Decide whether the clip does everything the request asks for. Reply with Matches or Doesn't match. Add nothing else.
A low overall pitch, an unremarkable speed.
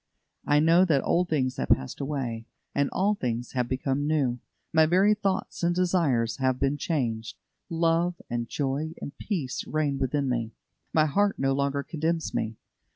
Doesn't match